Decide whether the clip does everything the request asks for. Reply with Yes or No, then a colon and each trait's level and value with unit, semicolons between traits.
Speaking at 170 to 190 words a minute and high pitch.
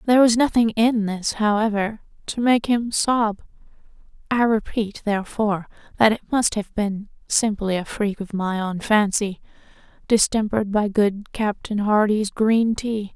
No: average, 145 wpm; high, 215 Hz